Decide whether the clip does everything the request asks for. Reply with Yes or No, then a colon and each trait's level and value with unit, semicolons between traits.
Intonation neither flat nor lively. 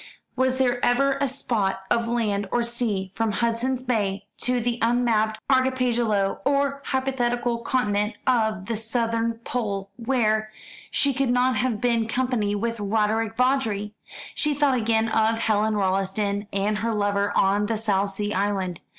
Yes: average, 3.1 semitones